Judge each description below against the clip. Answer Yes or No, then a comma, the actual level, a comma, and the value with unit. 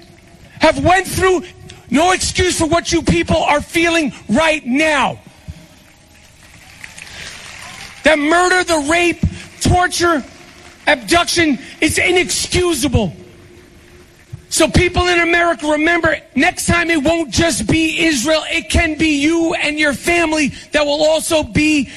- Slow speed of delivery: Yes, slow, 120 wpm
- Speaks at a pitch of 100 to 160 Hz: No, very high, 320 Hz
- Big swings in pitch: No, narrow, 2.5 semitones